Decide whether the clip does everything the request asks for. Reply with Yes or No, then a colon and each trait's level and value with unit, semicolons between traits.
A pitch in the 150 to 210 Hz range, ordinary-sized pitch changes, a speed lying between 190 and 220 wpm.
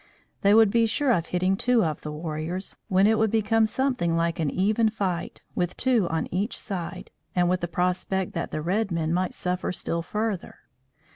Yes: medium, 185 Hz; average, 4.3 semitones; average, 195 wpm